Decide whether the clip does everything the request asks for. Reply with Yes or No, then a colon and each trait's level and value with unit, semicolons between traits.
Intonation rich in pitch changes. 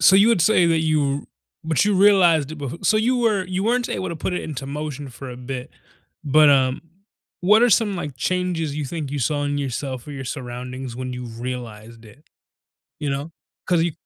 Yes: wide, 5.7 semitones